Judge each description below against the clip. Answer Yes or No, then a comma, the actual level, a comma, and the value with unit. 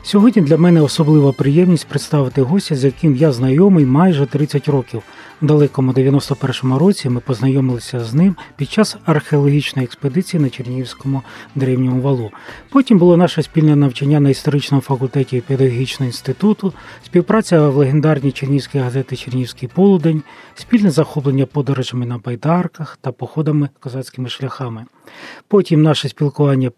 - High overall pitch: No, medium, 140 Hz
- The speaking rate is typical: Yes, average, 135 wpm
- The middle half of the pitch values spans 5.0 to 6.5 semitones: No, average, 3.2 semitones